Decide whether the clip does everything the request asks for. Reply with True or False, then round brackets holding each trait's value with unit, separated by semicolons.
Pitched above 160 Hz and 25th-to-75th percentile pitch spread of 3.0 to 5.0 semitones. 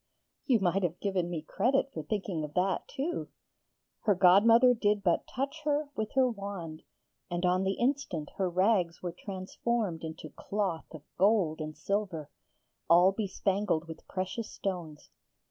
True (190 Hz; 4.2 semitones)